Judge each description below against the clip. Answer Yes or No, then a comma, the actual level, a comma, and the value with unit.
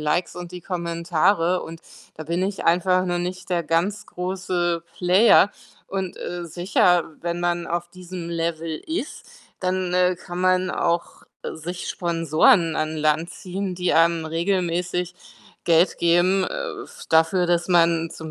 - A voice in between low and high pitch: Yes, medium, 175 Hz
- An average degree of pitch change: No, narrow, 1.6 semitones